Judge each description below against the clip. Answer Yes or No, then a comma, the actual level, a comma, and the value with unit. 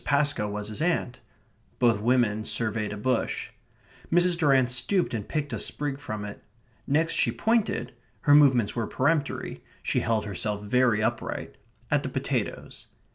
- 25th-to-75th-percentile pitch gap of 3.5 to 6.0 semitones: Yes, average, 5.2 semitones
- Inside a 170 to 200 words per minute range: No, average, 150 wpm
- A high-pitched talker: No, low, 125 Hz